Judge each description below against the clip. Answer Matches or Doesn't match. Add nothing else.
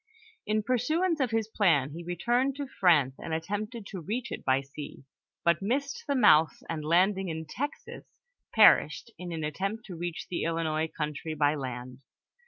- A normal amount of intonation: Doesn't match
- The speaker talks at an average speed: Matches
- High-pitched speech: Doesn't match